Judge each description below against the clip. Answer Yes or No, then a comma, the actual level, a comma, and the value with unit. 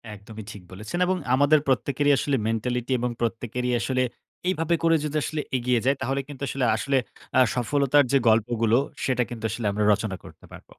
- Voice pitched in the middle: No, low, 125 Hz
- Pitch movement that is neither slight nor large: Yes, average, 3.8 semitones